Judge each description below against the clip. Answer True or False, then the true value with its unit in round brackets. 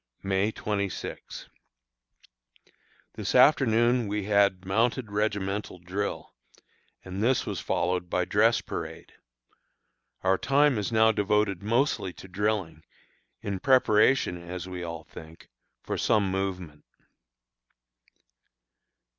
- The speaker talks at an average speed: False (105 wpm)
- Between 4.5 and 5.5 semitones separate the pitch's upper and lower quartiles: False (3.1 semitones)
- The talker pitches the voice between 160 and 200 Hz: False (100 Hz)